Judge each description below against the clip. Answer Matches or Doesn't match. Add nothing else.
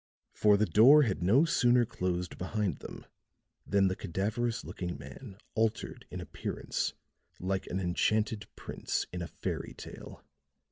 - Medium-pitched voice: Doesn't match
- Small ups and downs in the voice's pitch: Doesn't match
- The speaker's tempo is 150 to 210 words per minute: Doesn't match